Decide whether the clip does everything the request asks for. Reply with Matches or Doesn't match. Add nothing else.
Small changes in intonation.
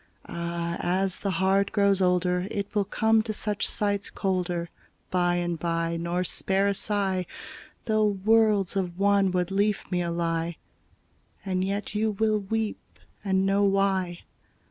Matches